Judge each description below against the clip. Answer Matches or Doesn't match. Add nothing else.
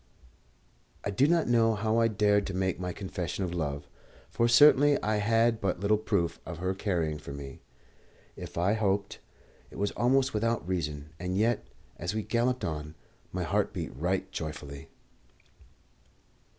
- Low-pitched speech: Matches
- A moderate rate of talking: Matches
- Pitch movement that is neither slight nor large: Matches